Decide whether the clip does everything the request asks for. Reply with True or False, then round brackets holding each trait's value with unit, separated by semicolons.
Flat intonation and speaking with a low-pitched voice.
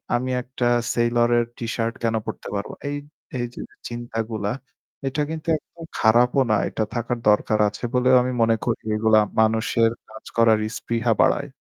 True (1.7 semitones; 115 Hz)